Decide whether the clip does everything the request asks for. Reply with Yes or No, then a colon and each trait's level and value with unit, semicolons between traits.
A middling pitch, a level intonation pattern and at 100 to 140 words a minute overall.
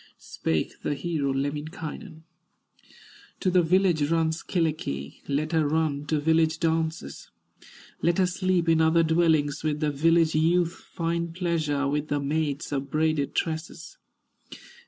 Yes: medium, 160 Hz; narrow, 2.2 semitones; slow, 135 wpm